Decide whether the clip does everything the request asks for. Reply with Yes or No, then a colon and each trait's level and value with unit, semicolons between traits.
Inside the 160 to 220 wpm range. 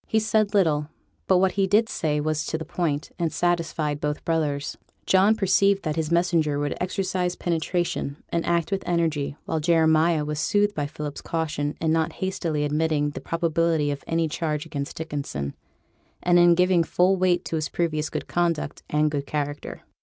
Yes: average, 175 wpm